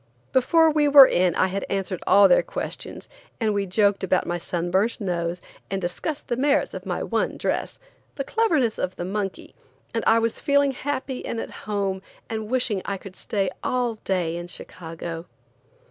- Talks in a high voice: Yes, high, 200 Hz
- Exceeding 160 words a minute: Yes, average, 180 wpm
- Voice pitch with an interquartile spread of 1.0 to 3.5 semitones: No, wide, 5.5 semitones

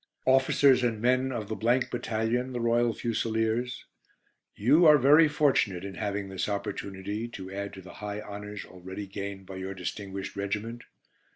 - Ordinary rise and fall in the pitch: Yes, average, 3.6 semitones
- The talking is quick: No, average, 155 wpm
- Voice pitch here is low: Yes, low, 110 Hz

